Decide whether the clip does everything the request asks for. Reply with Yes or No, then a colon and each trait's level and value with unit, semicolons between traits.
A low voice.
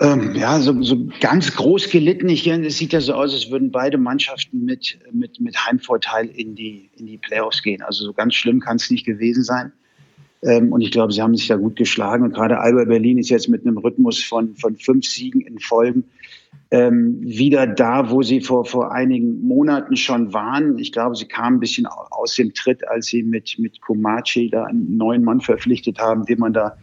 Yes: low, 130 Hz